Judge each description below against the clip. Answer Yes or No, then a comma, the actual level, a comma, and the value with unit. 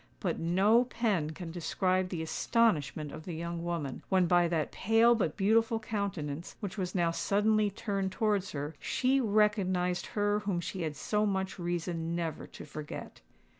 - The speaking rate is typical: Yes, average, 165 wpm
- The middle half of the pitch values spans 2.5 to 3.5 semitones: No, average, 3.9 semitones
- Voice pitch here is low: No, medium, 185 Hz